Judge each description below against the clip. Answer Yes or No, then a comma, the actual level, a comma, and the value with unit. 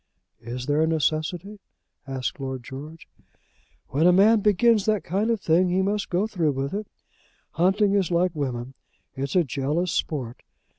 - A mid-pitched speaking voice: Yes, medium, 170 Hz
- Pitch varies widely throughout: Yes, wide, 6.0 semitones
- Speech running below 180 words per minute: Yes, average, 160 wpm